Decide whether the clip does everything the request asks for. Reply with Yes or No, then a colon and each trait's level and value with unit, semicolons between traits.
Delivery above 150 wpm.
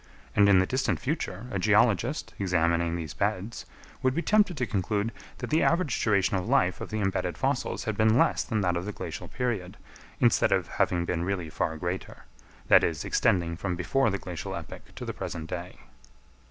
Yes: average, 195 wpm